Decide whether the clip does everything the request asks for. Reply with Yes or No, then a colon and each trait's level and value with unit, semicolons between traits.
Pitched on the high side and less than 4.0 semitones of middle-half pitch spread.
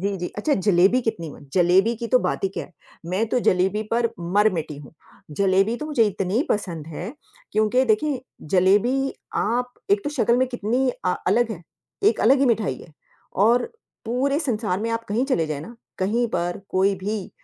No: high, 210 Hz; average, 4.5 semitones